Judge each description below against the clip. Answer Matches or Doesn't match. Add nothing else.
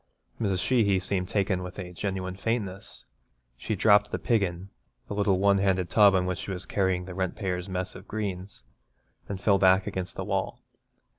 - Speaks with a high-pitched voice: Doesn't match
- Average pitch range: Doesn't match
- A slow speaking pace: Doesn't match